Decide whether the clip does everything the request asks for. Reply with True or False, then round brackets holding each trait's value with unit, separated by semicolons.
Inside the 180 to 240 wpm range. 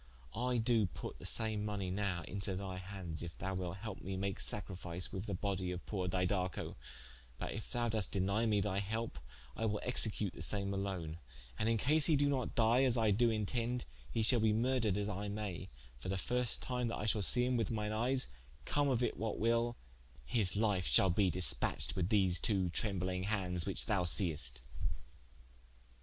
True (195 wpm)